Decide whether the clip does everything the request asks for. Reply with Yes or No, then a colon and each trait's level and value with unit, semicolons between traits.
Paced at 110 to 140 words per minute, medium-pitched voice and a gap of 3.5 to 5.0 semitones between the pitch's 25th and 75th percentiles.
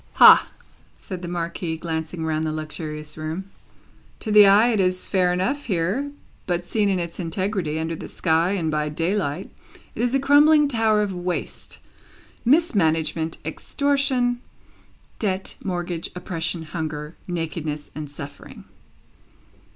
Yes: slow, 135 wpm; medium, 175 Hz; average, 4.6 semitones